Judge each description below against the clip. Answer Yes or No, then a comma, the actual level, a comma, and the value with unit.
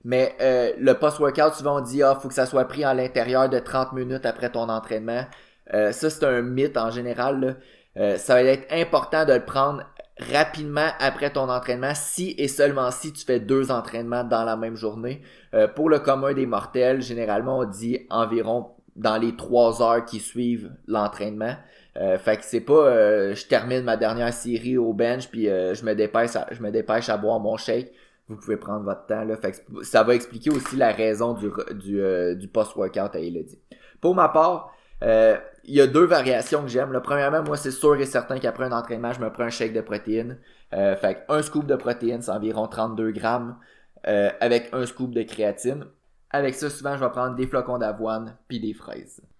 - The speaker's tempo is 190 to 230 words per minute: Yes, average, 205 wpm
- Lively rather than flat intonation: No, average, 3.6 semitones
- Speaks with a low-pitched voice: Yes, low, 125 Hz